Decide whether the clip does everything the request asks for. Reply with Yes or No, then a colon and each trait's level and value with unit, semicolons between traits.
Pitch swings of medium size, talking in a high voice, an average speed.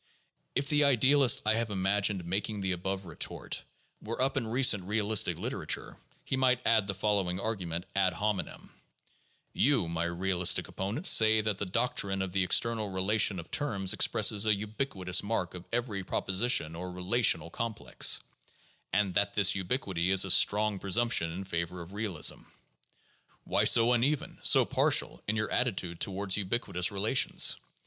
No: average, 3.8 semitones; low, 100 Hz; average, 155 wpm